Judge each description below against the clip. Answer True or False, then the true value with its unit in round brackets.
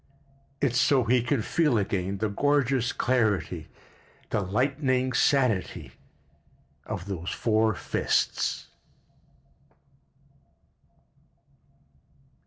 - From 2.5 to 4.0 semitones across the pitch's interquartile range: False (4.6 semitones)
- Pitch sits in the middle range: False (120 Hz)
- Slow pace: True (75 wpm)